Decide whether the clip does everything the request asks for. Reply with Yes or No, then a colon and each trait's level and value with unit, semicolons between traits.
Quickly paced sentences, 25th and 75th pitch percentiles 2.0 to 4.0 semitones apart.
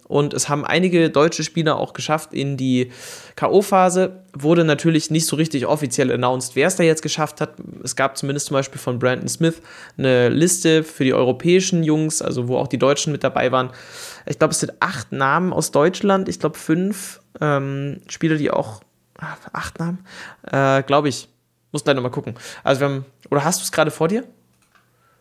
Yes: fast, 195 wpm; average, 3.3 semitones